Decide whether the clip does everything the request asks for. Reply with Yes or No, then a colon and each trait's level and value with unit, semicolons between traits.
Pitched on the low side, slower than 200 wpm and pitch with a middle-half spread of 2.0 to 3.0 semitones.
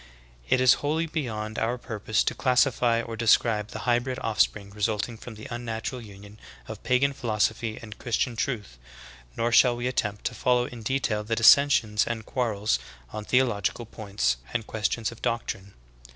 Yes: low, 115 Hz; average, 165 wpm; narrow, 2.6 semitones